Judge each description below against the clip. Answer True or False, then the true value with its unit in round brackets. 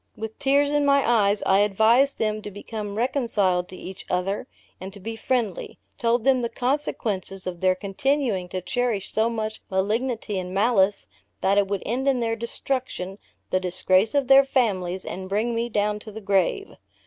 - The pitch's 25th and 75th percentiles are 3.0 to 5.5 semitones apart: True (4.2 semitones)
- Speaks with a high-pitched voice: True (215 Hz)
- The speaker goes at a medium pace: True (180 wpm)